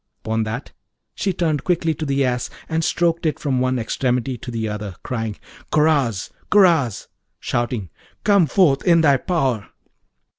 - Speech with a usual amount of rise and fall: No, wide, 5.7 semitones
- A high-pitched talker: No, low, 135 Hz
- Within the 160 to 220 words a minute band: No, average, 150 wpm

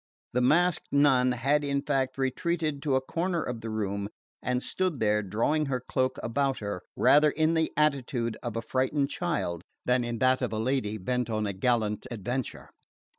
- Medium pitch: No, low, 130 Hz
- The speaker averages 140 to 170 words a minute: No, average, 180 wpm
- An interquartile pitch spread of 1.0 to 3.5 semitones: No, average, 4.0 semitones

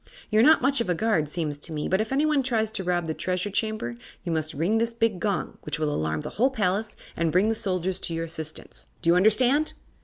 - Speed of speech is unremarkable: No, fast, 240 wpm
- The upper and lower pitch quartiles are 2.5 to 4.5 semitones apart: No, wide, 5.4 semitones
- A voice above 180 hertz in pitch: Yes, high, 190 Hz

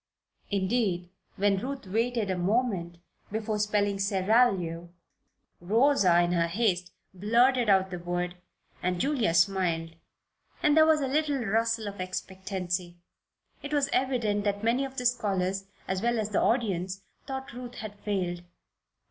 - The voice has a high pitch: Yes, high, 205 Hz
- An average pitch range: Yes, average, 4.7 semitones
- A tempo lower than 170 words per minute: Yes, average, 140 wpm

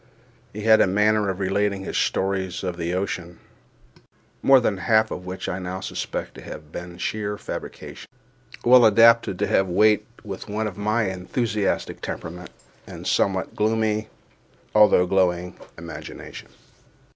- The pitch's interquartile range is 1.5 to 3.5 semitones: Yes, average, 3.0 semitones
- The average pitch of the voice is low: Yes, low, 100 Hz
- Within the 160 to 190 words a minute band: No, average, 145 wpm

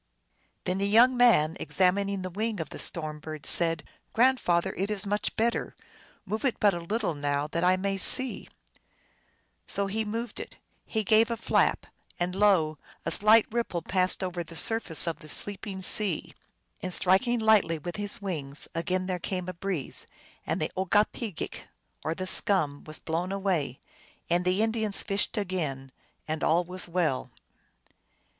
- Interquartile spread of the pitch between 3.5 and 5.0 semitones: Yes, average, 3.9 semitones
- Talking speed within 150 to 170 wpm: Yes, average, 165 wpm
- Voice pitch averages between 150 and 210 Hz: Yes, medium, 185 Hz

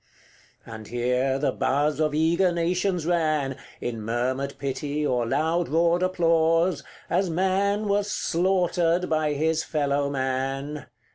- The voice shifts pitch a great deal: No, average, 4.2 semitones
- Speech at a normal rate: No, slow, 130 wpm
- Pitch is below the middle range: No, medium, 155 Hz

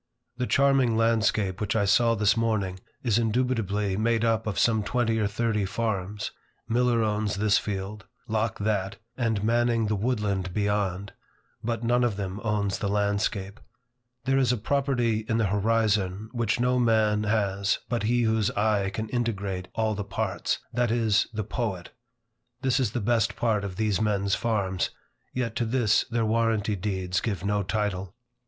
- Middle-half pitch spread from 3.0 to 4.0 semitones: No, narrow, 2.4 semitones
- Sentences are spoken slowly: No, average, 165 wpm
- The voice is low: Yes, low, 110 Hz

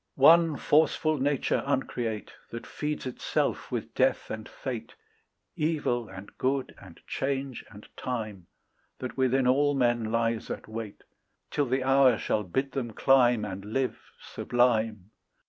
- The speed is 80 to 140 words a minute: Yes, slow, 135 wpm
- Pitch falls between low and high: No, low, 125 Hz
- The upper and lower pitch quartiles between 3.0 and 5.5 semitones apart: Yes, average, 3.5 semitones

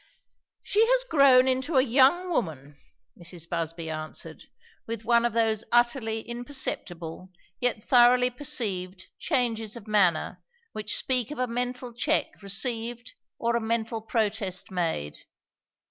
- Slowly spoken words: Yes, slow, 130 wpm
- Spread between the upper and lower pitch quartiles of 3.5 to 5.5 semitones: Yes, average, 4.5 semitones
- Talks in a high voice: Yes, high, 230 Hz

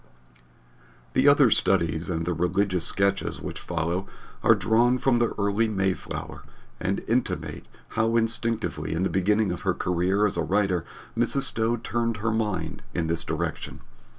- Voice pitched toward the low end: Yes, low, 100 Hz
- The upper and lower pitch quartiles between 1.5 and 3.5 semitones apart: No, average, 4.2 semitones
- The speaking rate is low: No, average, 150 wpm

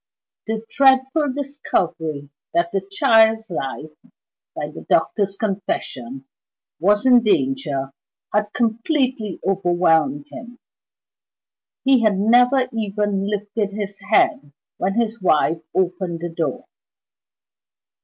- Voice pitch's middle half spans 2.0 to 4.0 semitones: No, average, 5.1 semitones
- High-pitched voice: Yes, high, 205 Hz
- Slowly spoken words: Yes, slow, 105 wpm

